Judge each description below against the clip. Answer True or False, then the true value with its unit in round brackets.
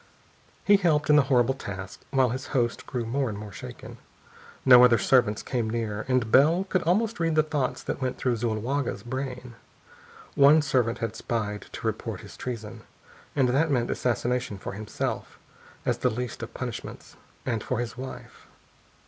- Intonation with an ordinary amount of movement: True (3.3 semitones)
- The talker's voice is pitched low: True (125 Hz)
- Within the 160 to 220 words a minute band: True (170 wpm)